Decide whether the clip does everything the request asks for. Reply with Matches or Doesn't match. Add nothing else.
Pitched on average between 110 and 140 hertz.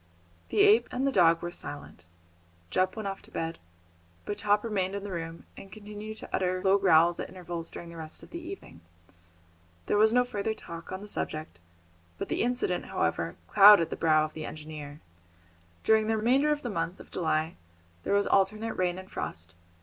Doesn't match